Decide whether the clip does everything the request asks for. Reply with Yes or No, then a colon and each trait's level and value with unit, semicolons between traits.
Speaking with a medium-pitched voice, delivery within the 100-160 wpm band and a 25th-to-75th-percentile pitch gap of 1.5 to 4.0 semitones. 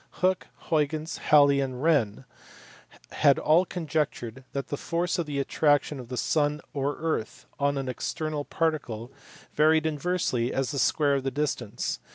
Yes: medium, 145 Hz; average, 155 wpm; average, 2.7 semitones